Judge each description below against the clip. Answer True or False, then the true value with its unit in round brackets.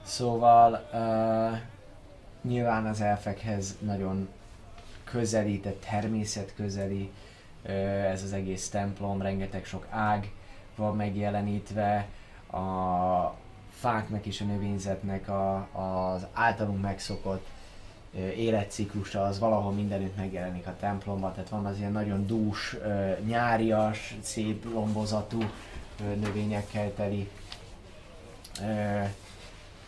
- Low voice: True (100 Hz)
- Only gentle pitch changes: True (1.6 semitones)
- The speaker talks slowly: True (100 wpm)